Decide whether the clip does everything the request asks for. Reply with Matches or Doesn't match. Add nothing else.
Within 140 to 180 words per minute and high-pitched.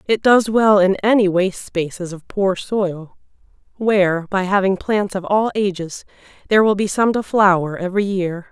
Matches